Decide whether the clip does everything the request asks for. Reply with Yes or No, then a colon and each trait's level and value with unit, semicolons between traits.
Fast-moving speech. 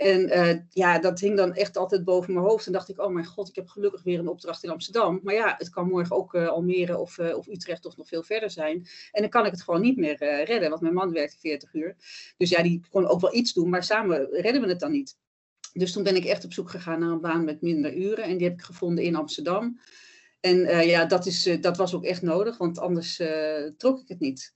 Yes: fast, 275 wpm